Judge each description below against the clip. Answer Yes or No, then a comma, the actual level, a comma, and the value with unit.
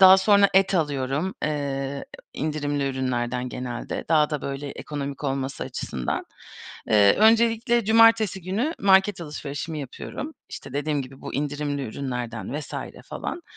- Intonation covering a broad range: Yes, wide, 6.0 semitones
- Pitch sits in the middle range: Yes, medium, 145 Hz